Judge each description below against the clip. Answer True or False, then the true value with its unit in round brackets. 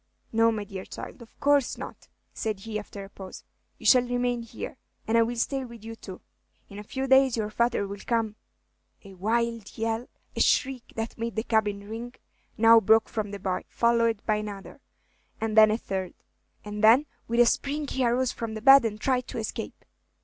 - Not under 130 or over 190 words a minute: False (200 wpm)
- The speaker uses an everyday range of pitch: False (2.2 semitones)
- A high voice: True (225 Hz)